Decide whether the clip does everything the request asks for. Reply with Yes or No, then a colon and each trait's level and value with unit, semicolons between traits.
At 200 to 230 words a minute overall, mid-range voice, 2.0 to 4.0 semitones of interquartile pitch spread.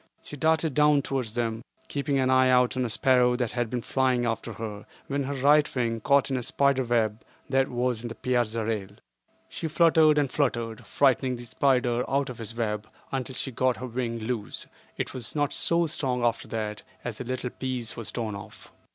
No: fast, 205 wpm; low, 125 Hz; average, 2.9 semitones